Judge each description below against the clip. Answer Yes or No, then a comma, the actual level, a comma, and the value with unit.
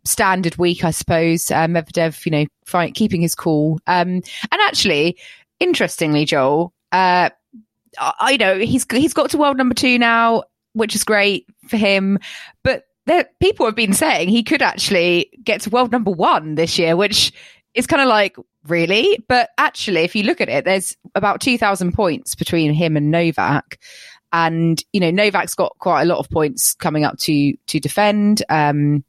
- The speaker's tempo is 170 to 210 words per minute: Yes, average, 180 wpm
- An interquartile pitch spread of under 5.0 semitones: No, wide, 5.4 semitones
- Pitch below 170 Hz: No, high, 190 Hz